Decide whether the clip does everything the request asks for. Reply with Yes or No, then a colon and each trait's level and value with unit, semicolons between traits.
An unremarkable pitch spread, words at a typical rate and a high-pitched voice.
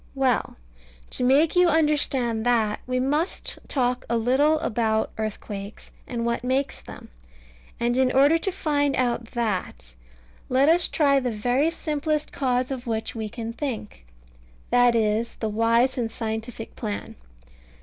Yes: average, 3.7 semitones; average, 145 wpm; high, 245 Hz